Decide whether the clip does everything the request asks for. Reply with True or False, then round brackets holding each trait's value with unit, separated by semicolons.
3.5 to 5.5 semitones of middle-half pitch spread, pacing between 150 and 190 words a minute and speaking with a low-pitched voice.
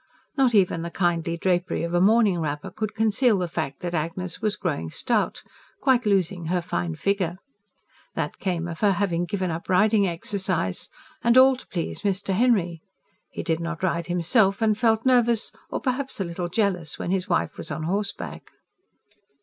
False (4.0 semitones; 175 wpm; 185 Hz)